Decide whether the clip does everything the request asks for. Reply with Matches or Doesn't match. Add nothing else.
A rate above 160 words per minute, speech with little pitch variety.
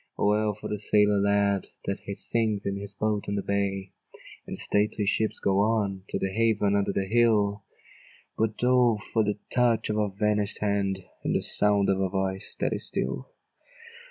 Matches